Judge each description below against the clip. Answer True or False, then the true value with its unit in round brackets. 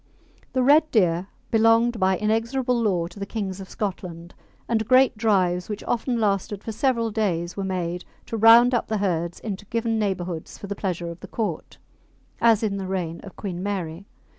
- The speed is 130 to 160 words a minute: False (185 wpm)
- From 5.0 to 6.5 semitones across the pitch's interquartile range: False (3.9 semitones)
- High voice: True (205 Hz)